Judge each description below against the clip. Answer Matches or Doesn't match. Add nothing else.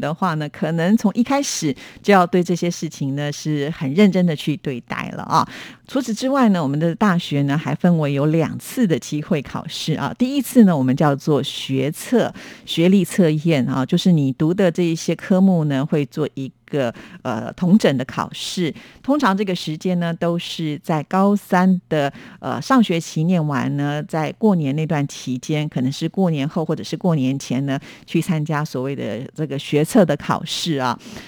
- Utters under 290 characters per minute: Matches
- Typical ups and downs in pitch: Matches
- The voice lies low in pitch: Doesn't match